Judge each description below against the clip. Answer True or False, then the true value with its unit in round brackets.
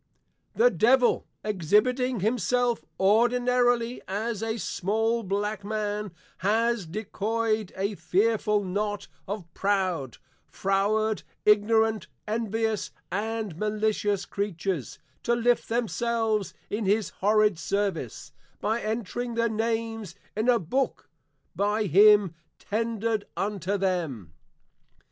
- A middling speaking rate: False (100 wpm)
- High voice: True (215 Hz)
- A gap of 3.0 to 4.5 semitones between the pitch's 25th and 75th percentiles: False (2.4 semitones)